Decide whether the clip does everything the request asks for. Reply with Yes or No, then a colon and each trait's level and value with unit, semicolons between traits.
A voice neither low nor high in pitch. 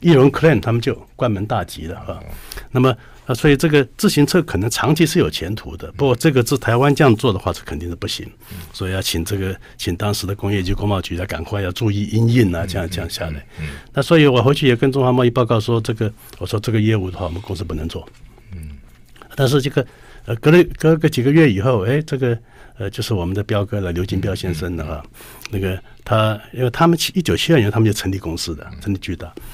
No: low, 110 Hz